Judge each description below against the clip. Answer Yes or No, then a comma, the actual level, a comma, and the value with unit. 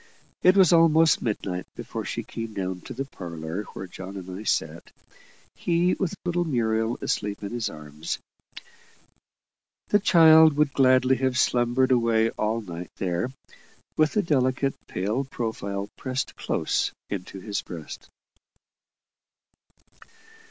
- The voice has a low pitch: Yes, low, 115 Hz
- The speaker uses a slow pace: Yes, slow, 130 wpm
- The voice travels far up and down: Yes, wide, 6.2 semitones